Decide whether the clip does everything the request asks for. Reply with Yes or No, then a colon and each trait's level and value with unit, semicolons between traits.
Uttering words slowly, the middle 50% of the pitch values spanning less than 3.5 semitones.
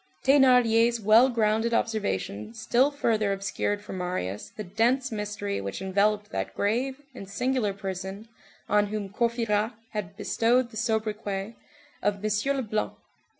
Yes: slow, 130 wpm; average, 2.8 semitones